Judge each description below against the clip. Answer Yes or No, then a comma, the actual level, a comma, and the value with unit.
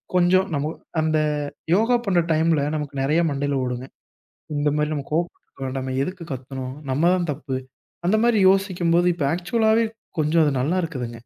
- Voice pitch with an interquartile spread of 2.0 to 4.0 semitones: No, average, 4.4 semitones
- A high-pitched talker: No, medium, 160 Hz